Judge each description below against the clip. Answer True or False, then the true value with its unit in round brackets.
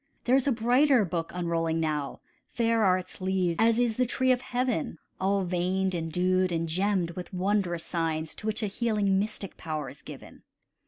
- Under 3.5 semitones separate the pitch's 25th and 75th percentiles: False (4.7 semitones)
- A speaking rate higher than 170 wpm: True (190 wpm)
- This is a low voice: False (185 Hz)